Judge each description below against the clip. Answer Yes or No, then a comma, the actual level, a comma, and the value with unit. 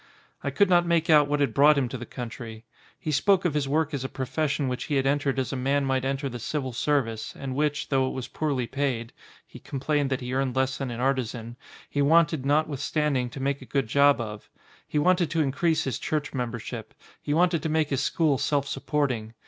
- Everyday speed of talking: No, fast, 225 wpm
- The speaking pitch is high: No, medium, 140 Hz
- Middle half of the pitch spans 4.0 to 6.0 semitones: No, average, 2.7 semitones